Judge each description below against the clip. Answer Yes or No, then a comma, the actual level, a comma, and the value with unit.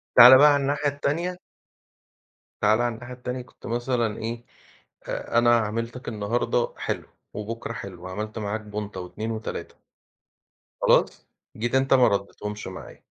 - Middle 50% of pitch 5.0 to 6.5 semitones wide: No, average, 2.9 semitones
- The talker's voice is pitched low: Yes, low, 115 Hz